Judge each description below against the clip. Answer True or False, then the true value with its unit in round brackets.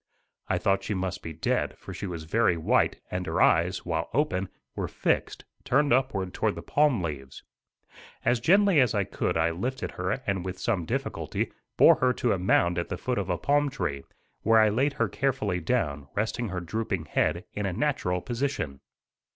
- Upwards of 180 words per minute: True (190 wpm)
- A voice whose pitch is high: False (95 Hz)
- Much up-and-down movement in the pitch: True (6.4 semitones)